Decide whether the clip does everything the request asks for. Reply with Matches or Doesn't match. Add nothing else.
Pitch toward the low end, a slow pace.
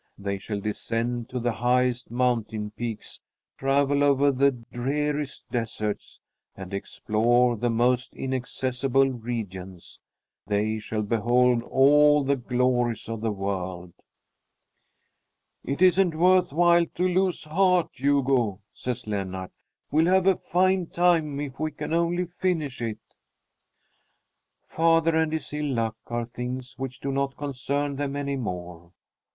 Matches